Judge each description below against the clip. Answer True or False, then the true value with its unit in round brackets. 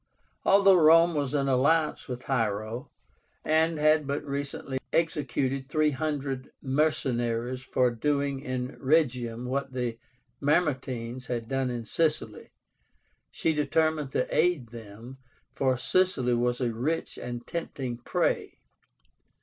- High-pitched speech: False (135 Hz)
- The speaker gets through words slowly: True (115 wpm)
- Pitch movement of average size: True (3.7 semitones)